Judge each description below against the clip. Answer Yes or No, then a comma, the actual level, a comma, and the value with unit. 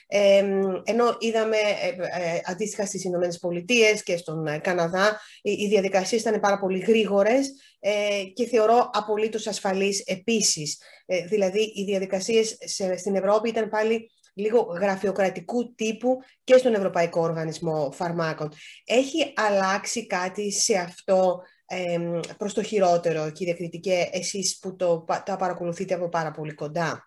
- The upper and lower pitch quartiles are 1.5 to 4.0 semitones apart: Yes, average, 3.4 semitones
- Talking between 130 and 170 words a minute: No, average, 120 wpm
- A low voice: No, high, 195 Hz